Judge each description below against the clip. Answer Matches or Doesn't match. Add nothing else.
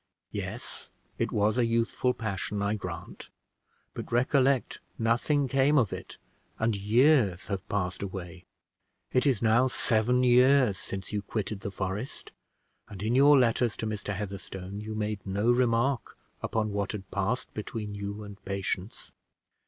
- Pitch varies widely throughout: Doesn't match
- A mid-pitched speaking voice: Doesn't match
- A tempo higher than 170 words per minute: Doesn't match